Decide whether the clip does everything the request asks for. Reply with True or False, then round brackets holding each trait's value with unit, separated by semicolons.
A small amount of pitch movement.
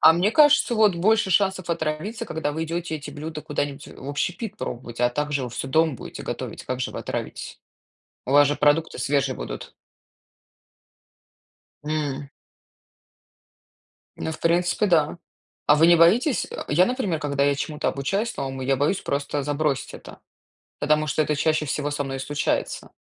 False (3.3 semitones)